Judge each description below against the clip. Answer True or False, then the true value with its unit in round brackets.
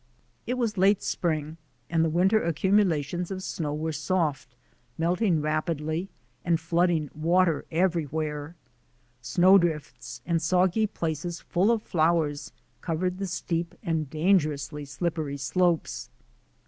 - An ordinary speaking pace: False (120 wpm)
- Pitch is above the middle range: False (165 Hz)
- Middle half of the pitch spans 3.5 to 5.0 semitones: False (2.9 semitones)